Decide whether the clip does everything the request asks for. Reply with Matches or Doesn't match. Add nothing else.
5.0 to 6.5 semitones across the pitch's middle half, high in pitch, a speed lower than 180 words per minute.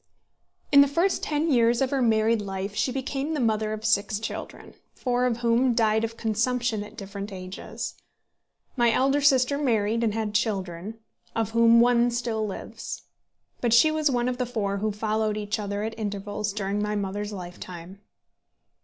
Doesn't match